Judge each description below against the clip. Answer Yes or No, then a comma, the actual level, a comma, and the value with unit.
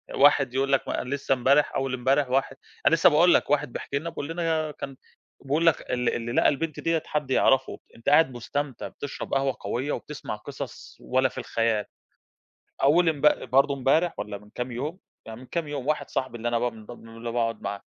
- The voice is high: No, low, 135 Hz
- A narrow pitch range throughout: No, average, 3.5 semitones